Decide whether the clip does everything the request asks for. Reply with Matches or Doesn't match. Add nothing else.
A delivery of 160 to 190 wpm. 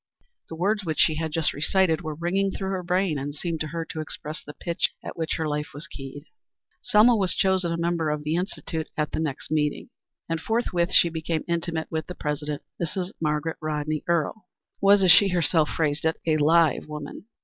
Doesn't match